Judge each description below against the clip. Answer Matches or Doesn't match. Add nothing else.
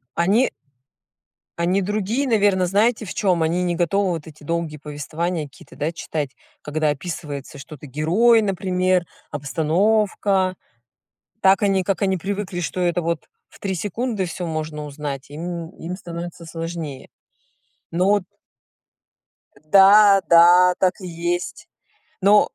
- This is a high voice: Doesn't match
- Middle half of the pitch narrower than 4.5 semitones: Matches